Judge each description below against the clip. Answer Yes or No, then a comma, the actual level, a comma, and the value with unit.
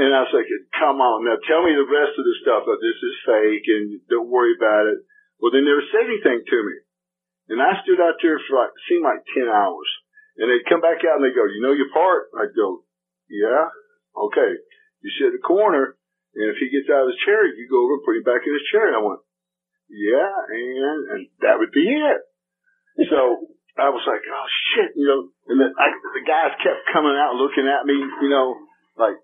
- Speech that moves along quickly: Yes, fast, 230 wpm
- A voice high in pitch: Yes, very high, 355 Hz